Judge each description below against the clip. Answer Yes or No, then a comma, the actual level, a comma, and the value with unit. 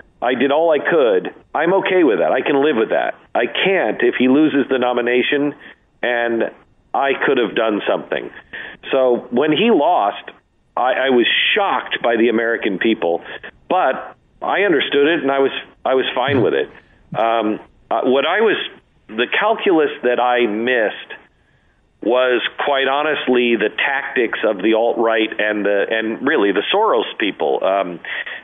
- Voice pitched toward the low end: Yes, low, 125 Hz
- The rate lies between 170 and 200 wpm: No, average, 160 wpm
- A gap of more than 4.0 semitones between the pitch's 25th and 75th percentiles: No, average, 3.5 semitones